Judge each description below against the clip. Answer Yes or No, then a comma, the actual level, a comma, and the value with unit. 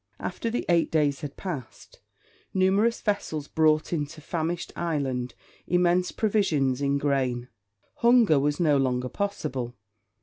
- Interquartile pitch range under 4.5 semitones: No, average, 4.9 semitones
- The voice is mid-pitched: Yes, medium, 155 Hz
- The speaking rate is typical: No, slow, 125 wpm